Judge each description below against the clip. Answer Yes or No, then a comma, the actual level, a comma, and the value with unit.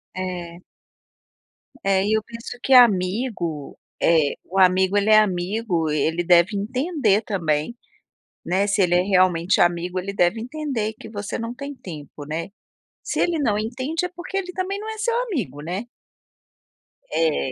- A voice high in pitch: Yes, high, 200 Hz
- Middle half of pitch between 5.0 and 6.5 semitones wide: Yes, wide, 5.6 semitones